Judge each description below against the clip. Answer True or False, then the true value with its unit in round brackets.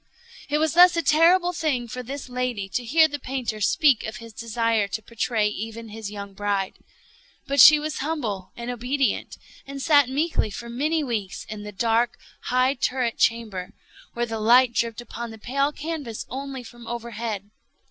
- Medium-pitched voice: False (240 Hz)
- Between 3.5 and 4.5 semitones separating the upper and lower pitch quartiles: True (4.0 semitones)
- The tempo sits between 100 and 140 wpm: False (175 wpm)